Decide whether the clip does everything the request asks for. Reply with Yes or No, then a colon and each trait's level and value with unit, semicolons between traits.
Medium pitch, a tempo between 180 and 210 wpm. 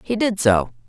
Yes: medium, 165 Hz; fast, 205 wpm